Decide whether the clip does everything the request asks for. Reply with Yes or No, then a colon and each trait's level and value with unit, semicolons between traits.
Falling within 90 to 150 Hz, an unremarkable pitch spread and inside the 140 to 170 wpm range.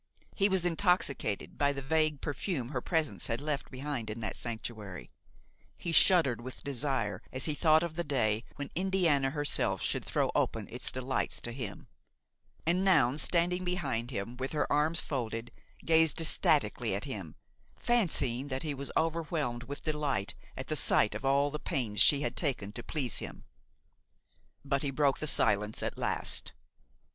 Yes: medium, 140 Hz; average, 4.7 semitones; average, 165 wpm